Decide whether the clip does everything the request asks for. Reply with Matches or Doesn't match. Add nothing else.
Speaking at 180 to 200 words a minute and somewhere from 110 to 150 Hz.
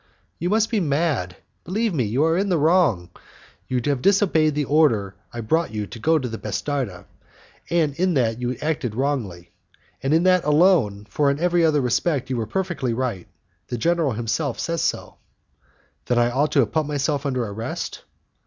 Matches